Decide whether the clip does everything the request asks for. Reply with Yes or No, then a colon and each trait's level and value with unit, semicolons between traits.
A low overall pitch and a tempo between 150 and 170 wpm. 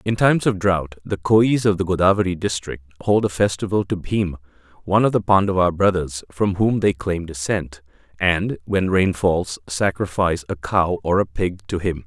No: very low, 90 Hz; average, 185 wpm